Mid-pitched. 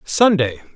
Yes: medium, 155 Hz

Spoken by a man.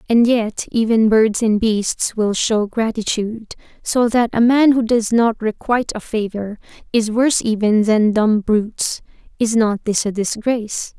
No: female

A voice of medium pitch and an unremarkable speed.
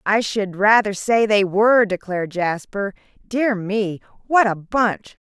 No: high, 205 Hz; average, 150 wpm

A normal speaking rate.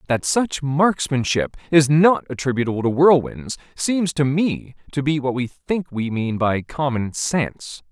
Yes: average, 160 wpm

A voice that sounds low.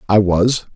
Yes: low, 100 Hz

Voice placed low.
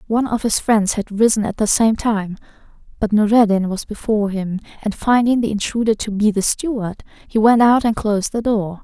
No: high, 215 Hz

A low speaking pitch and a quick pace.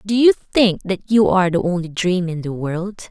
No: high, 190 Hz; fast, 230 wpm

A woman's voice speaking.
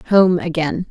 Yes: female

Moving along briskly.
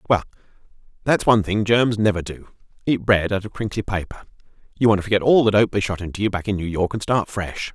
Yes: fast, 240 wpm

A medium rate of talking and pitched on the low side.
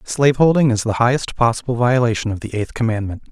Yes: average, 180 wpm; low, 120 Hz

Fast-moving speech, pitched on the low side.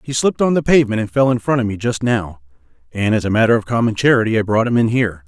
Yes: fast, 285 wpm; low, 120 Hz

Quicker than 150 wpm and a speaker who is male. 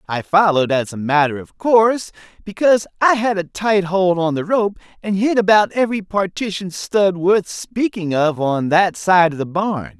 Yes: average, 185 wpm; male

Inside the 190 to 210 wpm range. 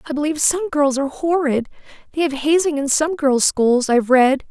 Yes: average, 200 wpm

